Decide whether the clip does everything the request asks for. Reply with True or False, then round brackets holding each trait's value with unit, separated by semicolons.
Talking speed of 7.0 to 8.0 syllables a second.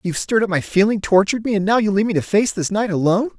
True (7.7 syllables/s)